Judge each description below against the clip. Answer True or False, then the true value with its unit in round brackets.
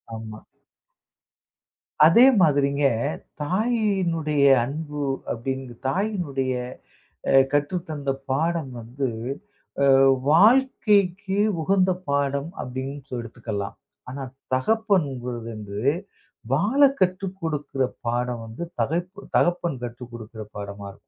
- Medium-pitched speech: True (145 Hz)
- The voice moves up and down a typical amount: False (6.6 semitones)